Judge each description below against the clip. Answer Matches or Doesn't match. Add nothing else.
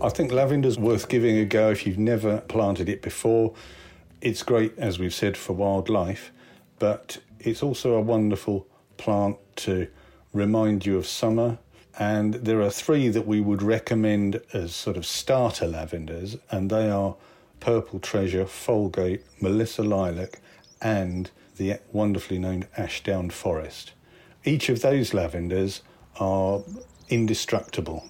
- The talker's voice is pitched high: Doesn't match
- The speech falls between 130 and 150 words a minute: Matches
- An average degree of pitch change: Matches